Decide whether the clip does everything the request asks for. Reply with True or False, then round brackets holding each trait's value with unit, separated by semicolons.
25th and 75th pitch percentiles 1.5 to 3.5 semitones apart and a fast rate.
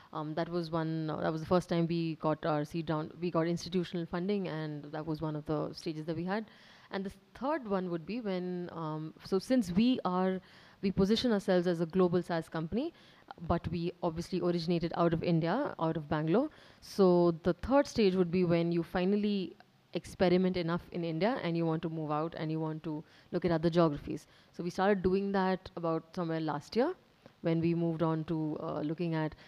True (2.5 semitones; 210 wpm)